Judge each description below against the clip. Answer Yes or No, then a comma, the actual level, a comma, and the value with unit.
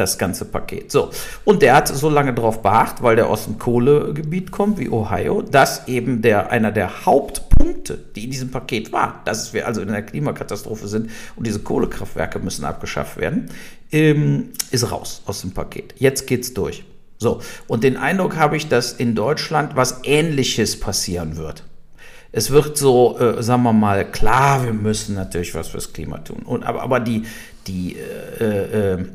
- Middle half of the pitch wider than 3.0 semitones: Yes, average, 5.2 semitones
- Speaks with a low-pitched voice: Yes, low, 120 Hz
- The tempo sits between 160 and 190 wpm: Yes, average, 180 wpm